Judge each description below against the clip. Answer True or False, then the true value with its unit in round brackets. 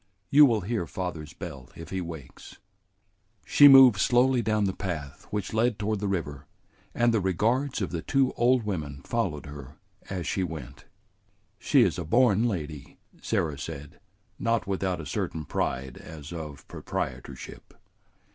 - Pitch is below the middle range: True (95 Hz)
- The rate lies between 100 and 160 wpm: True (155 wpm)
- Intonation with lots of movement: True (7.0 semitones)